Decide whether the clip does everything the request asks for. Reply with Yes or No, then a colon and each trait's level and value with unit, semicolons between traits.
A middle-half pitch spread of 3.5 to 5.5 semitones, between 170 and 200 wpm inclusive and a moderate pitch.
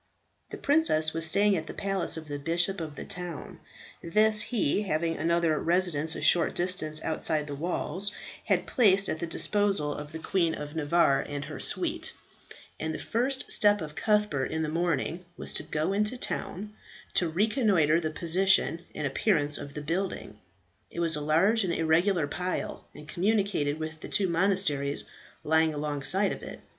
Yes: average, 4.1 semitones; average, 175 wpm; medium, 165 Hz